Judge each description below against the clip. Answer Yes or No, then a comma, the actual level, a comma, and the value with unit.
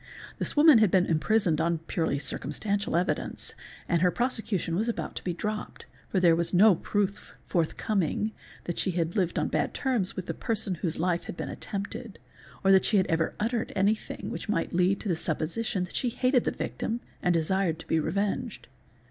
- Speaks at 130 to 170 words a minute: No, average, 190 wpm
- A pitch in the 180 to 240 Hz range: Yes, high, 190 Hz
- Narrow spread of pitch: No, average, 4.1 semitones